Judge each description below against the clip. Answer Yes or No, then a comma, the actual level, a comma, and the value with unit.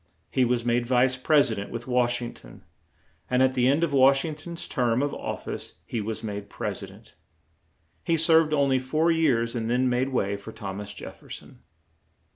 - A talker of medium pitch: No, low, 125 Hz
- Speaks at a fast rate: Yes, fast, 215 wpm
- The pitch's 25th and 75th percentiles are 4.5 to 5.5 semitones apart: No, average, 3.3 semitones